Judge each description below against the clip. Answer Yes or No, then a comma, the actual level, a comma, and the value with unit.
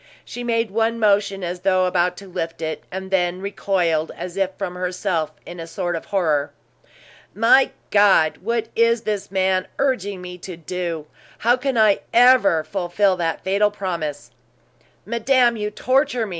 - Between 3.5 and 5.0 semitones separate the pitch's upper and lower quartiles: Yes, average, 3.9 semitones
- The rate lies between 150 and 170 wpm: Yes, average, 160 wpm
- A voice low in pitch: No, high, 190 Hz